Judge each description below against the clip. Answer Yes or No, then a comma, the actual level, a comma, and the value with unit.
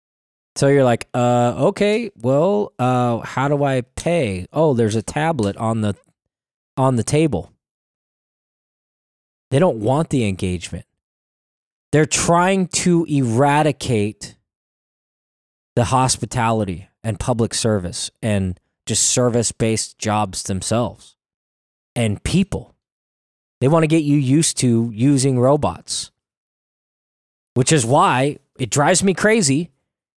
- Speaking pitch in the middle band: No, low, 120 Hz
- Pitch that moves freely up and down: Yes, wide, 5.9 semitones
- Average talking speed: No, slow, 115 wpm